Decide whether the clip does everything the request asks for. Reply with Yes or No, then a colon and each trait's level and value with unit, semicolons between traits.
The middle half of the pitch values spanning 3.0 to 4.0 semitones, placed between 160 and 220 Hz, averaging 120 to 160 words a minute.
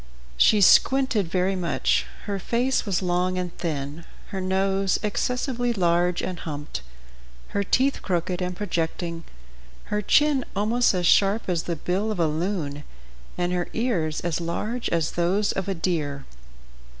Yes: average, 3.5 semitones; medium, 185 Hz; average, 150 wpm